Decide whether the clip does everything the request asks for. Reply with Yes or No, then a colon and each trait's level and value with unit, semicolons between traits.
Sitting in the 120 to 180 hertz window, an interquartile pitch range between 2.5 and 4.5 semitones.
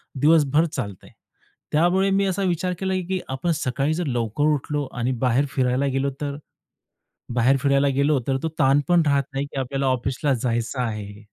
Yes: medium, 140 Hz; average, 3.2 semitones